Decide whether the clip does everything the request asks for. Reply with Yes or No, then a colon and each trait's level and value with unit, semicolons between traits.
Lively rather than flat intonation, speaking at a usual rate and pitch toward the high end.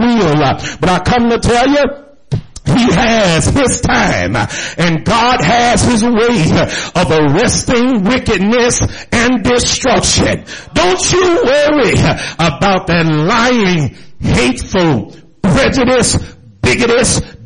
No: wide, 6.2 semitones; slow, 100 wpm; high, 230 Hz